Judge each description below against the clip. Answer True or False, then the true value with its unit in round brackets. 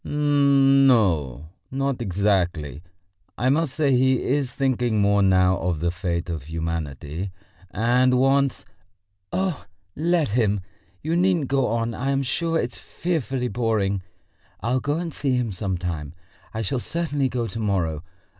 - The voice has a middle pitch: False (120 Hz)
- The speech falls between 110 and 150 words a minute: True (145 wpm)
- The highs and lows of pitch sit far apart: True (6.7 semitones)